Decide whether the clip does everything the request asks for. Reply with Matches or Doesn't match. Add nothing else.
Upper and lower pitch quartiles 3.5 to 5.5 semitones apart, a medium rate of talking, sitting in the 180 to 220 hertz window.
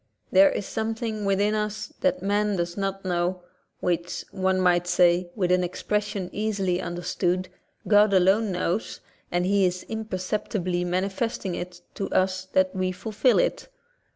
Doesn't match